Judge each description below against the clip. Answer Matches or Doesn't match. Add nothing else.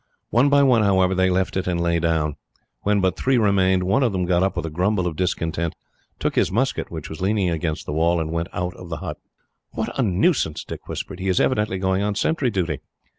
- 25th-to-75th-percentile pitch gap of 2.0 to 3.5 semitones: Matches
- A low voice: Matches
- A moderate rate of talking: Doesn't match